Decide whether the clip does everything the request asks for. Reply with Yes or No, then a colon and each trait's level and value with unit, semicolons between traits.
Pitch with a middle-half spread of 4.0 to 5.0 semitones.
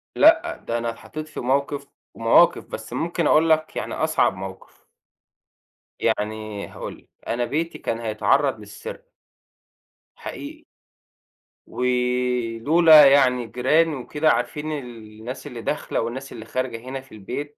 Yes: average, 4.4 semitones